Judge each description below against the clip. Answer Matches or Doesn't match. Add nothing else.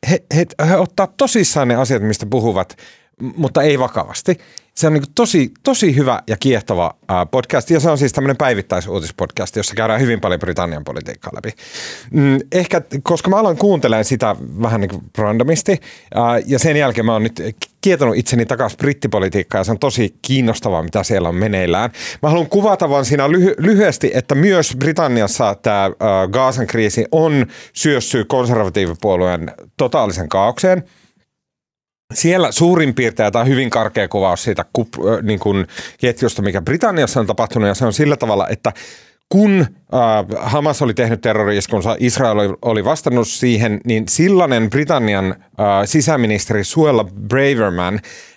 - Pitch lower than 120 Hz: Doesn't match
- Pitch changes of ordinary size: Doesn't match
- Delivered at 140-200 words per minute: Matches